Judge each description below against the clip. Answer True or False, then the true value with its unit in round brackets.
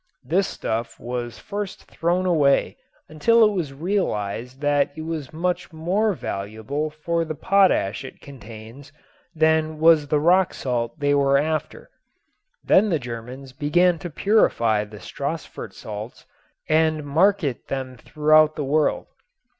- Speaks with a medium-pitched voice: True (150 Hz)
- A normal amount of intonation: True (4.5 semitones)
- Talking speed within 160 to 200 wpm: False (135 wpm)